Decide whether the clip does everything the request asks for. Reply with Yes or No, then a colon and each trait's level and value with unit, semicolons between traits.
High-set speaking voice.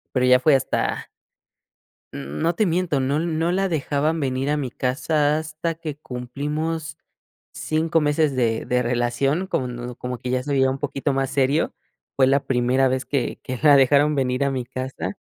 No: low, 135 Hz